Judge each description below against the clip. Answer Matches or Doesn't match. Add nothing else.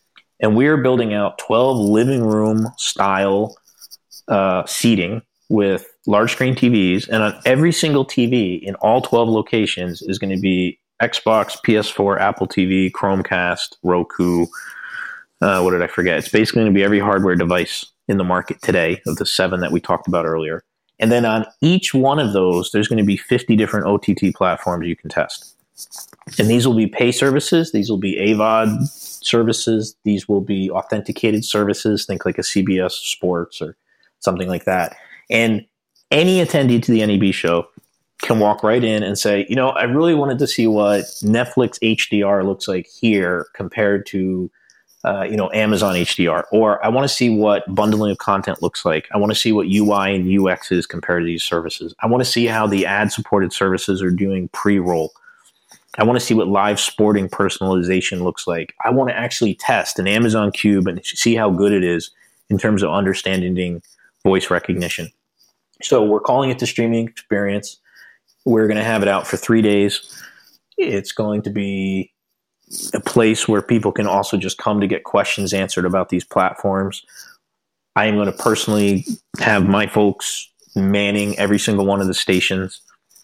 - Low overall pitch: Matches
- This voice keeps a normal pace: Matches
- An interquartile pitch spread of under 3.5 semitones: Matches